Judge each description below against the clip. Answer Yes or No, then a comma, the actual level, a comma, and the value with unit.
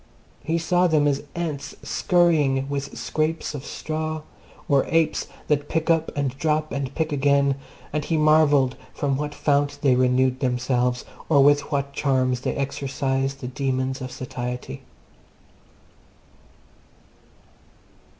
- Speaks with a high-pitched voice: No, medium, 140 Hz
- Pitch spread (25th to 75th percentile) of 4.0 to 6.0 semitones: No, narrow, 2.6 semitones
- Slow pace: Yes, slow, 130 wpm